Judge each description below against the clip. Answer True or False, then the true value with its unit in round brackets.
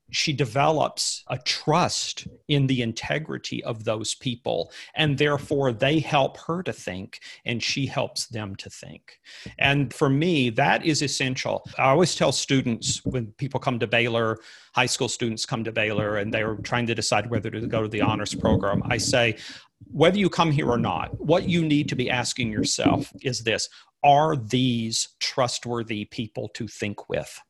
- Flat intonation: False (3.8 semitones)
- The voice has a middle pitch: False (125 Hz)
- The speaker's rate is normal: True (175 wpm)